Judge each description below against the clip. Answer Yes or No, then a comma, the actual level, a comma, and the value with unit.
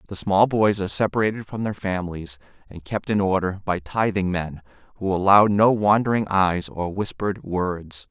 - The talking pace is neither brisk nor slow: Yes, average, 170 wpm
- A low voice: Yes, very low, 95 Hz